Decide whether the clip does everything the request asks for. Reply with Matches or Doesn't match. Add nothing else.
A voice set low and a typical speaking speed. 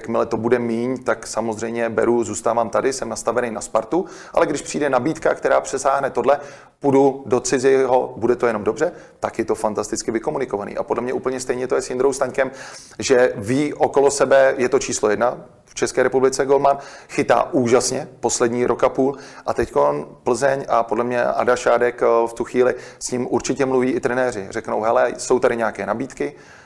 Doesn't match